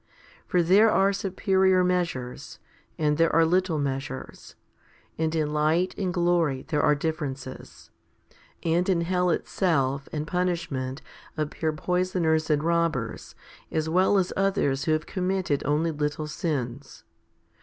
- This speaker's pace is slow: Yes, slow, 130 wpm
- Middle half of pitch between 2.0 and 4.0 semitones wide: Yes, average, 3.5 semitones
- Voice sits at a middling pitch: Yes, medium, 160 Hz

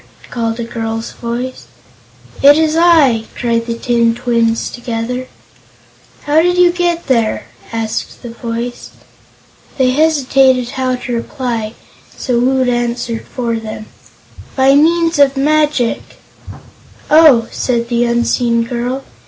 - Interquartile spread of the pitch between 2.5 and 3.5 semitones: Yes, average, 2.8 semitones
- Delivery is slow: Yes, slow, 120 wpm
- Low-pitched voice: No, high, 245 Hz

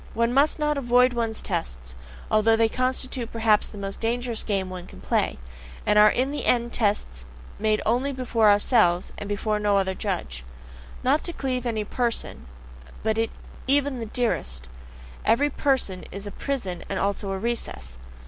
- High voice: Yes, high, 220 Hz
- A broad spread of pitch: No, average, 4.0 semitones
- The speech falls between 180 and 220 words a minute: No, average, 170 wpm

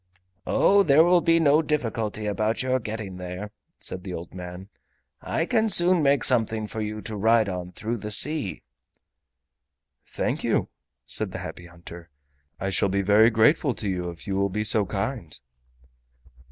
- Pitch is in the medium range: No, low, 110 Hz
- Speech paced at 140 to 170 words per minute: Yes, average, 165 wpm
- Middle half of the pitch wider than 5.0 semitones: Yes, wide, 5.5 semitones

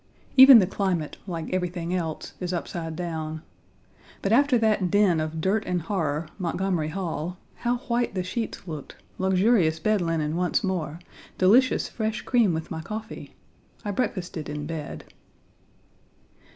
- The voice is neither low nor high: Yes, medium, 180 Hz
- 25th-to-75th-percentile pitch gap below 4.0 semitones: No, average, 4.6 semitones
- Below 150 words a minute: Yes, average, 140 wpm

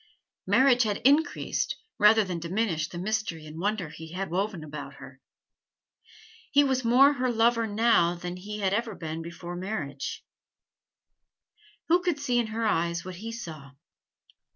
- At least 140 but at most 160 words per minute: Yes, average, 150 wpm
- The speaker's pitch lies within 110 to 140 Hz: No, high, 205 Hz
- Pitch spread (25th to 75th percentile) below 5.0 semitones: No, wide, 5.4 semitones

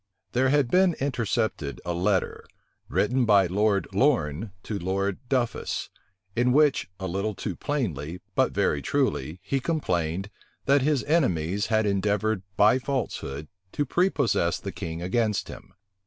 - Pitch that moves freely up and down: Yes, wide, 6.2 semitones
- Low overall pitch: Yes, low, 105 Hz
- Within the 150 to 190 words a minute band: No, average, 140 wpm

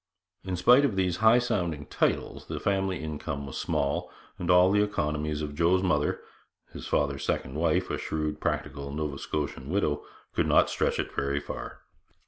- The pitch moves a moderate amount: Yes, average, 4.4 semitones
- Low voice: Yes, very low, 80 Hz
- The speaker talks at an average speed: Yes, average, 175 wpm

